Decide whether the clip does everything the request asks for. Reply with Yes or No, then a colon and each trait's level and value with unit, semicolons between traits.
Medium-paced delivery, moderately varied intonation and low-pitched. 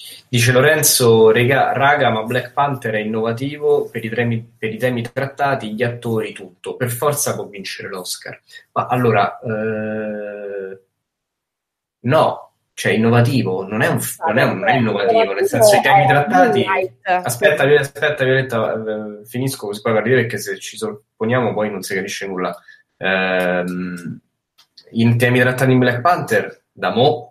Yes: average, 145 wpm; average, 4.4 semitones; low, 120 Hz